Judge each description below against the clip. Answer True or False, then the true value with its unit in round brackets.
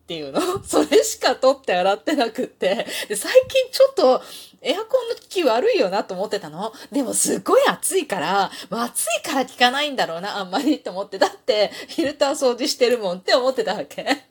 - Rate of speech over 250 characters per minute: True (405 characters per minute)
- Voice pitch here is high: True (275 Hz)